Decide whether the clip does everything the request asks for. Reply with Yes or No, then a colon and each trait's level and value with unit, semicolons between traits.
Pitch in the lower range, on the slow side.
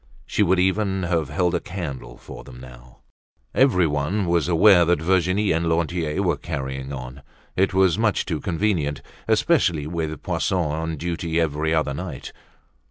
No: very low, 85 Hz; average, 155 wpm